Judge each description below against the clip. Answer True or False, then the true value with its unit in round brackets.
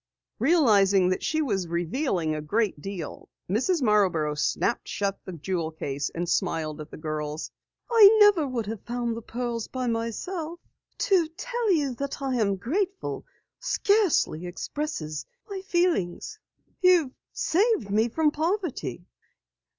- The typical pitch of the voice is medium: False (230 Hz)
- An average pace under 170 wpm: True (135 wpm)